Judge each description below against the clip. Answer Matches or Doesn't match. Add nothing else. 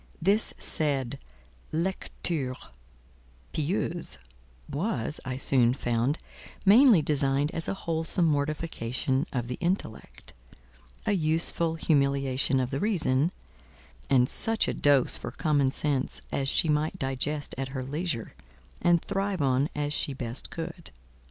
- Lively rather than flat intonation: Doesn't match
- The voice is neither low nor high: Matches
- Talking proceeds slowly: Matches